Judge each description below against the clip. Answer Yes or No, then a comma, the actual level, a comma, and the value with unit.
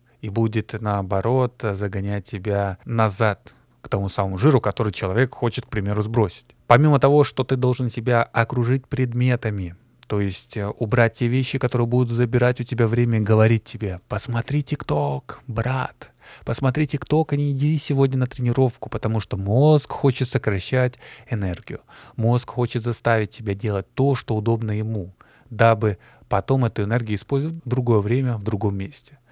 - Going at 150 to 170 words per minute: Yes, average, 155 wpm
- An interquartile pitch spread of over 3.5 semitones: No, average, 3.2 semitones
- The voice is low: Yes, low, 120 Hz